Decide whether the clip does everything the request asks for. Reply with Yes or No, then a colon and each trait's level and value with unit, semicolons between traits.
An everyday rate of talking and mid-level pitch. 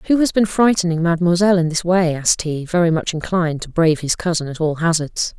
No: fast, 225 wpm; medium, 170 Hz